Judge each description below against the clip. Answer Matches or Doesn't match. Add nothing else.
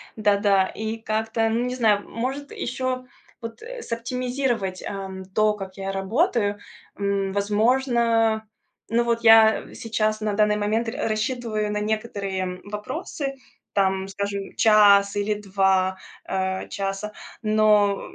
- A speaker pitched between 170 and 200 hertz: Doesn't match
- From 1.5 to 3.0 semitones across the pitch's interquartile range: Matches